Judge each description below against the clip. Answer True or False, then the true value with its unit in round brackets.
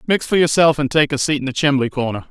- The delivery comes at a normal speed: False (285 wpm)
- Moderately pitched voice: True (145 Hz)